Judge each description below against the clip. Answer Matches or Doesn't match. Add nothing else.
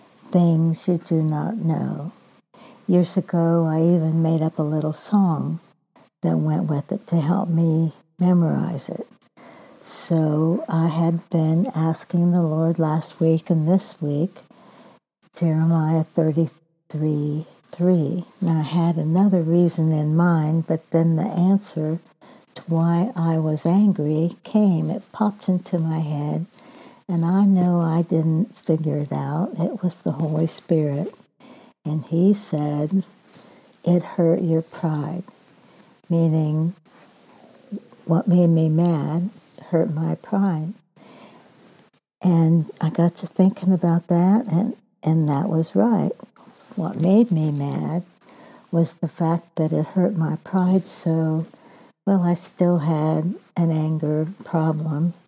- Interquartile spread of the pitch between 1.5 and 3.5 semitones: Matches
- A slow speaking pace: Matches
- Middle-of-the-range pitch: Matches